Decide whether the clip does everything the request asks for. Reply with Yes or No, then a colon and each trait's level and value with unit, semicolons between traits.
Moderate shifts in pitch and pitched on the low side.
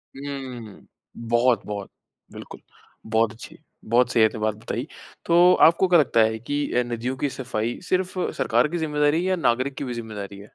Yes: average, 4.9 semitones; low, 125 Hz